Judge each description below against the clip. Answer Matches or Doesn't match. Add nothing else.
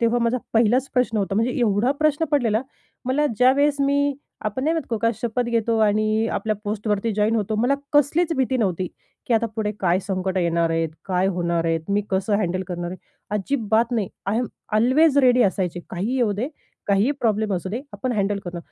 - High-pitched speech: Matches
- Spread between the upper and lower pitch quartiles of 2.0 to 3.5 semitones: Doesn't match